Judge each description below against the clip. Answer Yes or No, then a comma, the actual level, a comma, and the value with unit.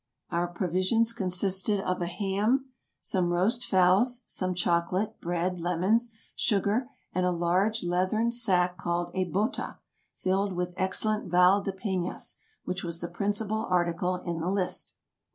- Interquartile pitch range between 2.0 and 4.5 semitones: Yes, average, 2.7 semitones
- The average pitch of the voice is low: No, medium, 185 Hz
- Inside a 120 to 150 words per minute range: Yes, average, 140 wpm